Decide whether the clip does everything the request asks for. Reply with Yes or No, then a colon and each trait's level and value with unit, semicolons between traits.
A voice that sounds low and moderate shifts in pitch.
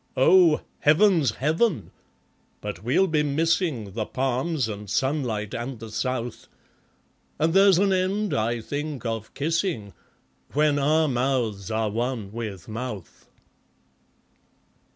No: low, 130 Hz; wide, 6.2 semitones